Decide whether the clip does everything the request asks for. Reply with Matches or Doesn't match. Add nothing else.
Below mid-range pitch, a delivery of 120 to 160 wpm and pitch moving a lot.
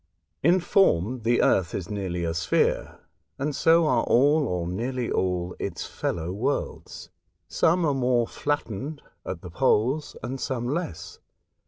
Matches